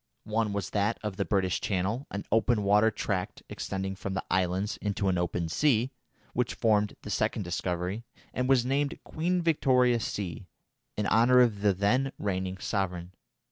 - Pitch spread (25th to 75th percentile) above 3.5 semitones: Yes, average, 4.0 semitones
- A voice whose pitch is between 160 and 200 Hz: No, low, 105 Hz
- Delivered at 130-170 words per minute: Yes, average, 165 wpm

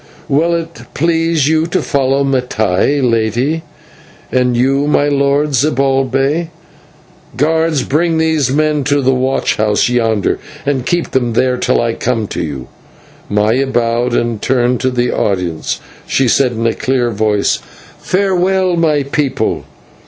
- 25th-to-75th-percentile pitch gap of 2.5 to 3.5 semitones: No, average, 4.1 semitones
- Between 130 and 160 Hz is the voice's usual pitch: Yes, low, 135 Hz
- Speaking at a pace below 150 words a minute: Yes, average, 140 wpm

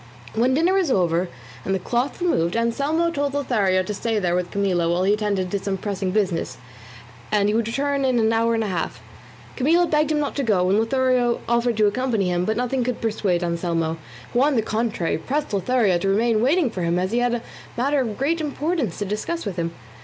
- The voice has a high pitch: Yes, high, 225 Hz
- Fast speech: Yes, fast, 220 wpm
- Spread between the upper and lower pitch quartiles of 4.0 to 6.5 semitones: Yes, wide, 5.6 semitones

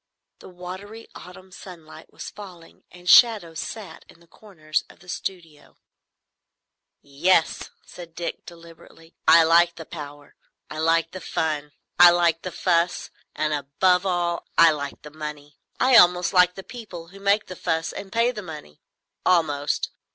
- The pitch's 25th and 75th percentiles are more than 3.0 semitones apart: No, narrow, 2.5 semitones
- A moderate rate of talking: Yes, average, 155 wpm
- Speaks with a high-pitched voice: No, medium, 170 Hz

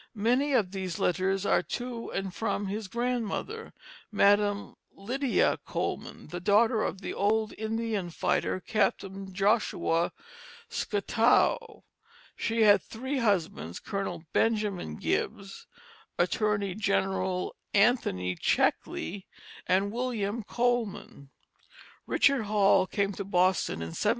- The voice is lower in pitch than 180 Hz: No, high, 205 Hz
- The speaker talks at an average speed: No, slow, 110 wpm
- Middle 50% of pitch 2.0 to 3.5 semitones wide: Yes, average, 3.0 semitones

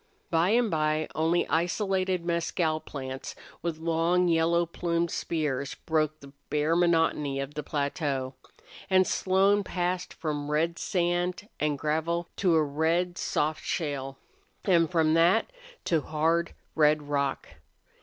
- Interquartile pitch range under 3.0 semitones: Yes, narrow, 2.6 semitones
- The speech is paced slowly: Yes, slow, 130 wpm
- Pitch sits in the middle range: Yes, medium, 165 Hz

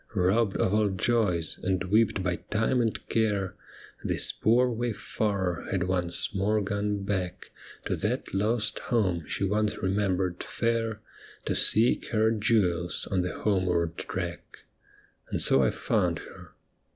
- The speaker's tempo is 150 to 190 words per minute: No, average, 140 wpm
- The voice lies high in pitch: No, low, 100 Hz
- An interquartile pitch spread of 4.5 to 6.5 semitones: No, average, 3.2 semitones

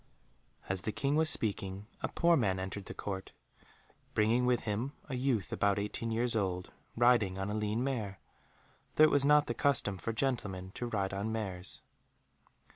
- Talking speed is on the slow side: No, average, 175 wpm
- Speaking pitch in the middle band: No, low, 110 Hz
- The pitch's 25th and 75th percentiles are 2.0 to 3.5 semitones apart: No, average, 4.3 semitones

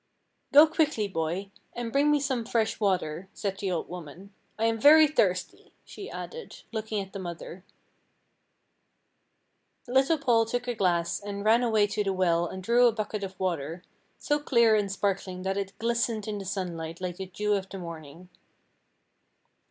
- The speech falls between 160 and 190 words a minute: Yes, average, 170 wpm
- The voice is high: Yes, high, 200 Hz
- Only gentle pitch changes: No, average, 4.2 semitones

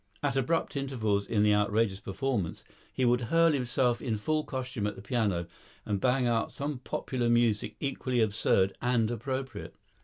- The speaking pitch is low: Yes, low, 120 Hz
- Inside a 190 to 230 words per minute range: No, average, 160 wpm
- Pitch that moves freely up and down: No, average, 3.9 semitones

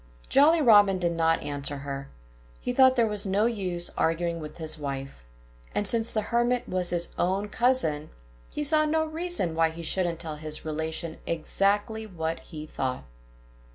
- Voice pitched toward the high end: No, medium, 175 Hz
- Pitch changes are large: Yes, wide, 6.1 semitones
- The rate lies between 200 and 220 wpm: No, average, 165 wpm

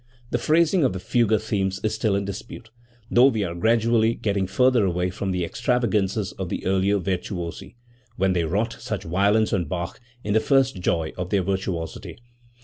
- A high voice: No, low, 100 Hz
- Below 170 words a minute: No, average, 180 wpm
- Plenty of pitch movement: No, average, 3.6 semitones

